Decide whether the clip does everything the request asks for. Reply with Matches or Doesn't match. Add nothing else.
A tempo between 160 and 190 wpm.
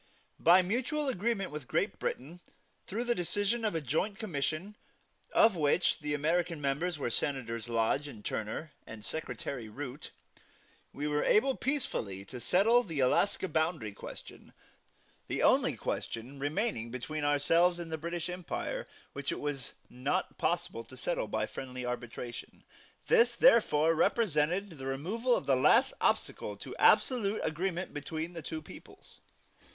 Doesn't match